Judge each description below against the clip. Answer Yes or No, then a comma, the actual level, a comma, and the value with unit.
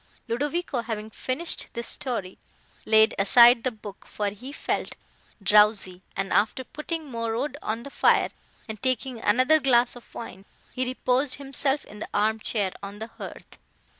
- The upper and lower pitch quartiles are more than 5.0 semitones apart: No, average, 3.6 semitones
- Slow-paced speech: No, average, 160 wpm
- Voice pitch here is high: Yes, high, 235 Hz